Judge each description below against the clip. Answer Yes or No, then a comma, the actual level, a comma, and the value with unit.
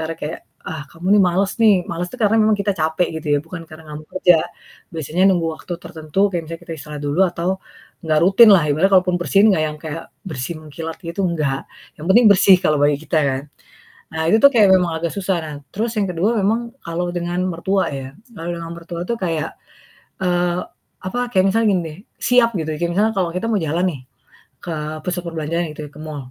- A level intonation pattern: No, average, 3.2 semitones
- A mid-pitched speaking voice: Yes, medium, 170 Hz